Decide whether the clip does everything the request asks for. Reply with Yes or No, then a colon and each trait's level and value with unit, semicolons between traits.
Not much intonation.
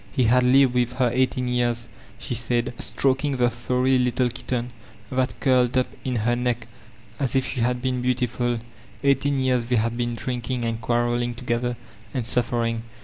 Yes: narrow, 1.2 semitones